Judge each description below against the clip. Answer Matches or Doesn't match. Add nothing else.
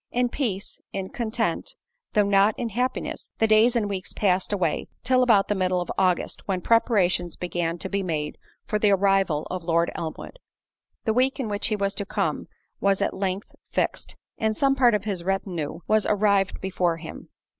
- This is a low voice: Doesn't match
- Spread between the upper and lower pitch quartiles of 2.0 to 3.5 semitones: Matches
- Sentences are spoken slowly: Doesn't match